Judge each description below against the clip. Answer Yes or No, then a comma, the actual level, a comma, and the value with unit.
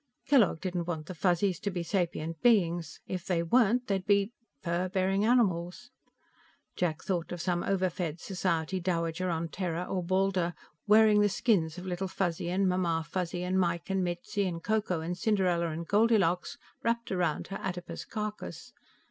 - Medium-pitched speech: Yes, medium, 180 Hz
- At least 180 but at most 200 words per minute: No, average, 165 wpm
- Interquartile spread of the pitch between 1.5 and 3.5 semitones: Yes, narrow, 2.5 semitones